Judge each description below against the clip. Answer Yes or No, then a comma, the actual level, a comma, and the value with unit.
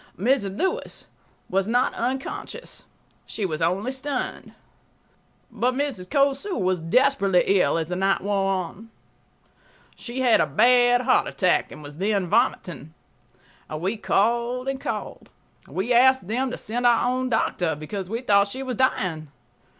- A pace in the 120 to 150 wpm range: Yes, average, 140 wpm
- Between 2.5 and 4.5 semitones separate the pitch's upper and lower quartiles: No, wide, 5.4 semitones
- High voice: Yes, high, 225 Hz